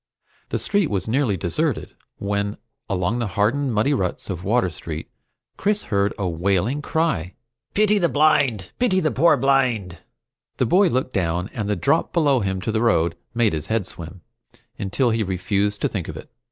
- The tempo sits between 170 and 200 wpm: Yes, average, 180 wpm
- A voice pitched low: Yes, low, 105 Hz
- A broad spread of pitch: Yes, wide, 6.6 semitones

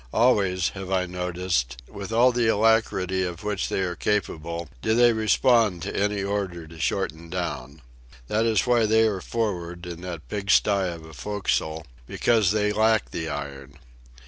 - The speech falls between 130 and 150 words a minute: No, average, 165 wpm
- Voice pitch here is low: Yes, very low, 95 Hz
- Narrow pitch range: No, average, 4.2 semitones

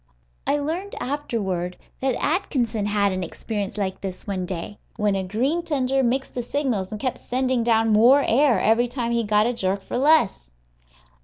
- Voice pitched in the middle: No, high, 230 Hz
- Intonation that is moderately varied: Yes, average, 4.9 semitones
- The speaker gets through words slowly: No, average, 175 wpm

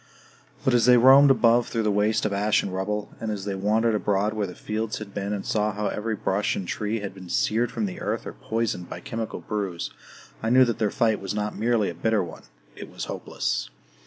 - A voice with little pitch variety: Yes, narrow, 2.3 semitones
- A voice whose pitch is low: Yes, low, 105 Hz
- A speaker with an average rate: No, fast, 230 wpm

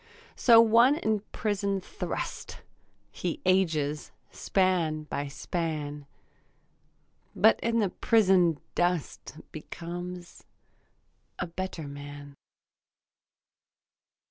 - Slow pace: Yes, slow, 80 wpm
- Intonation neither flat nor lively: Yes, average, 4.5 semitones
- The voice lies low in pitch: No, medium, 175 Hz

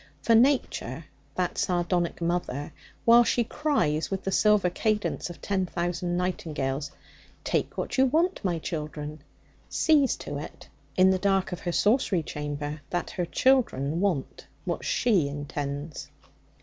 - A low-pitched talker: No, medium, 175 Hz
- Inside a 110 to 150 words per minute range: Yes, average, 140 wpm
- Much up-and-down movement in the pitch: Yes, wide, 5.7 semitones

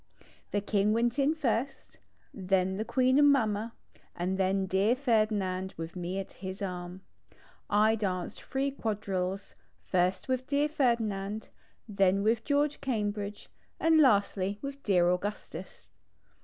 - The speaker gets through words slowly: Yes, slow, 130 wpm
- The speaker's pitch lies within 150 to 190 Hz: No, high, 205 Hz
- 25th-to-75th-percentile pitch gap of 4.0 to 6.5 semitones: Yes, average, 4.9 semitones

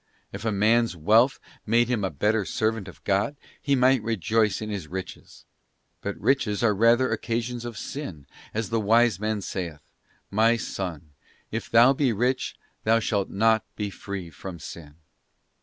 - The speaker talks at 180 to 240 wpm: No, average, 155 wpm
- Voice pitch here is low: Yes, low, 110 Hz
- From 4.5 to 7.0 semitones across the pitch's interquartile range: No, average, 3.1 semitones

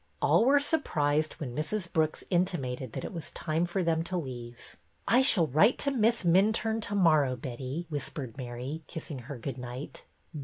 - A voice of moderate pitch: Yes, medium, 155 Hz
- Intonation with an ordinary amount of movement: No, wide, 6.3 semitones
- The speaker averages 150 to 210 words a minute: Yes, average, 175 wpm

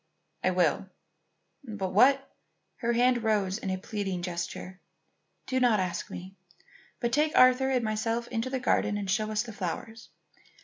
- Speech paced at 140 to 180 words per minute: Yes, average, 165 wpm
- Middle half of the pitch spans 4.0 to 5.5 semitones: Yes, average, 4.5 semitones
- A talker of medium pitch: No, high, 215 Hz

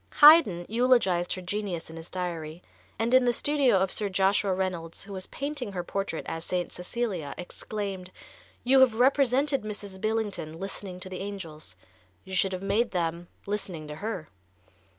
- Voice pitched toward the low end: No, high, 195 Hz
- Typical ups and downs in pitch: Yes, average, 4.2 semitones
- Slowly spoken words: No, average, 165 wpm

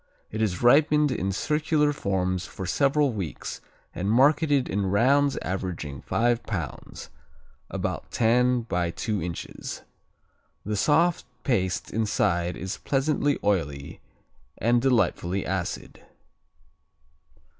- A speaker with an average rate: No, slow, 105 wpm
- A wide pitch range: Yes, wide, 6.8 semitones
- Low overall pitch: Yes, low, 110 Hz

